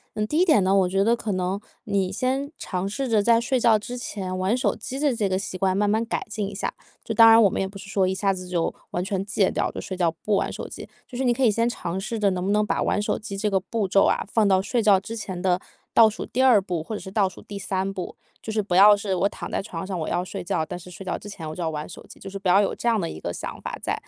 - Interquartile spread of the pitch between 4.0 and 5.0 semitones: No, average, 2.9 semitones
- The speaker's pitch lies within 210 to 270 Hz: No, high, 200 Hz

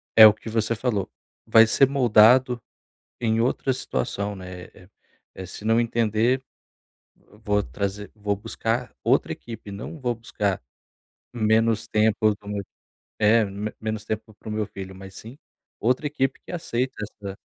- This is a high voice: No, low, 110 Hz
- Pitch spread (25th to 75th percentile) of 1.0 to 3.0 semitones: Yes, narrow, 2.4 semitones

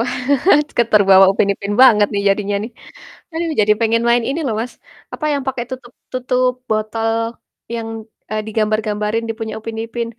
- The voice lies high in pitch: Yes, high, 225 Hz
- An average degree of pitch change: No, narrow, 2.3 semitones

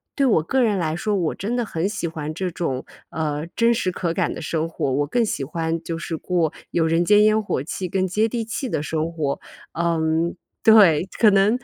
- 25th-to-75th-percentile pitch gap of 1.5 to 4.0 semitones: No, average, 4.7 semitones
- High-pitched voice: No, medium, 170 Hz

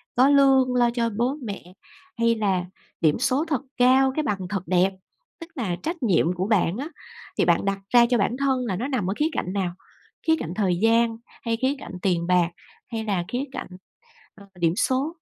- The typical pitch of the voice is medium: No, high, 230 Hz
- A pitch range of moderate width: No, wide, 5.7 semitones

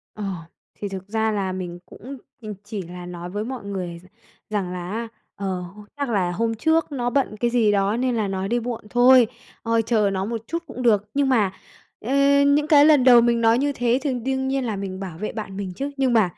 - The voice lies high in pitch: Yes, high, 225 Hz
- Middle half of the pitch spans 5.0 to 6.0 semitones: No, average, 4.3 semitones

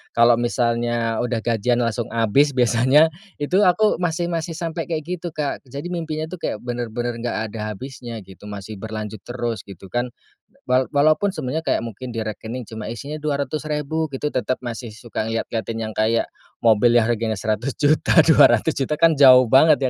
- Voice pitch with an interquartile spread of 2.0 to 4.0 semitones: No, average, 5.1 semitones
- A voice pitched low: Yes, low, 120 Hz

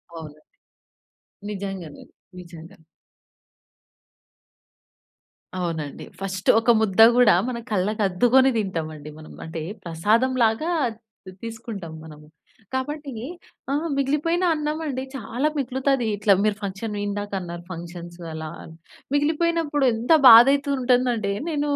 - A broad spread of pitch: Yes, wide, 7.3 semitones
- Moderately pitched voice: No, high, 220 Hz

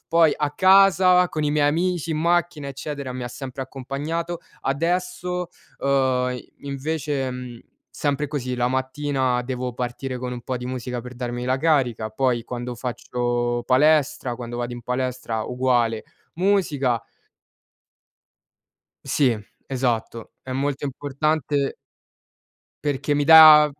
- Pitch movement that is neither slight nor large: Yes, average, 3.4 semitones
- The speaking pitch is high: No, low, 135 Hz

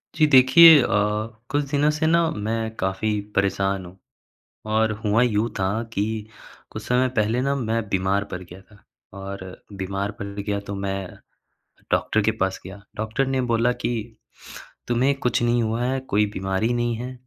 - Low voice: Yes, low, 110 Hz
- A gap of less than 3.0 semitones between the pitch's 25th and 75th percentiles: No, average, 4.1 semitones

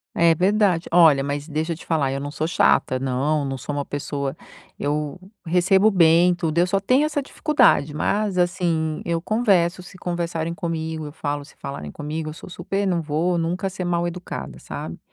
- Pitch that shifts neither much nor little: Yes, average, 3.4 semitones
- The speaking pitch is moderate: Yes, medium, 165 Hz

